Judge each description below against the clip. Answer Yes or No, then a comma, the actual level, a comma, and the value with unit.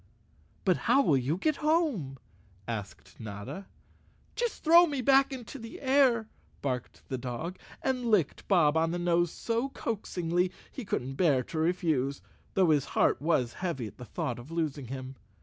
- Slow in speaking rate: No, average, 165 wpm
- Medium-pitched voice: Yes, medium, 170 Hz